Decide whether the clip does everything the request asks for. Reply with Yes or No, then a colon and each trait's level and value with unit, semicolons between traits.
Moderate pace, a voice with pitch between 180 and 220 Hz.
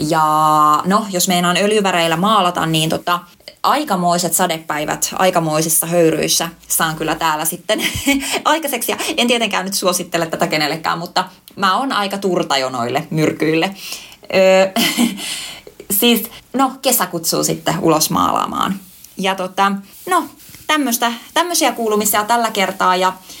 Yes: average, 120 wpm; medium, 185 Hz